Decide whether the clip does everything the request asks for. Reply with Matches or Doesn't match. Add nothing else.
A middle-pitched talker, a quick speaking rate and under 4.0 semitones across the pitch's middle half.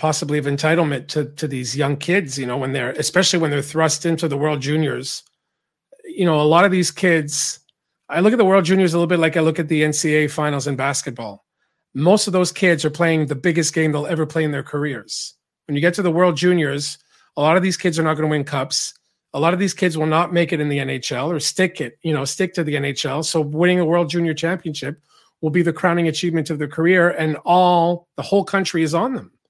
Matches